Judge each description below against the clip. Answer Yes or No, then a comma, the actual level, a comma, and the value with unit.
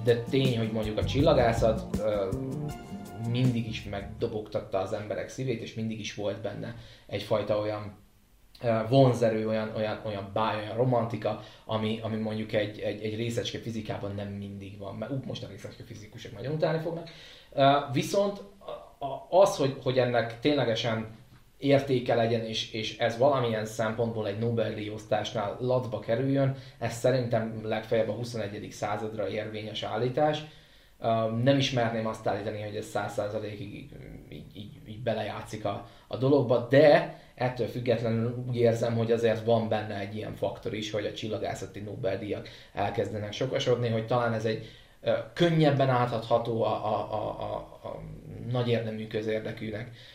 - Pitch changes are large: No, average, 2.7 semitones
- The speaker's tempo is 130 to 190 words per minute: Yes, average, 140 wpm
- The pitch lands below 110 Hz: No, low, 115 Hz